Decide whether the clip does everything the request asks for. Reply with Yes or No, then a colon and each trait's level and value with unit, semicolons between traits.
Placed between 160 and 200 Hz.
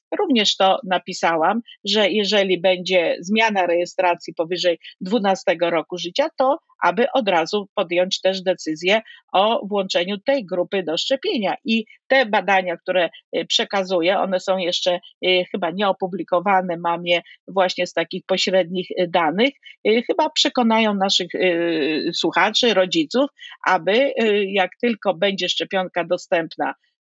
Yes: high, 190 Hz